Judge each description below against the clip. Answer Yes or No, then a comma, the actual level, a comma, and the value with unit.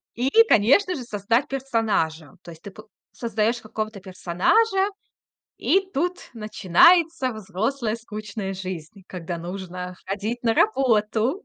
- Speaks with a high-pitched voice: Yes, high, 215 Hz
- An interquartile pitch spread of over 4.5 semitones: Yes, average, 5.3 semitones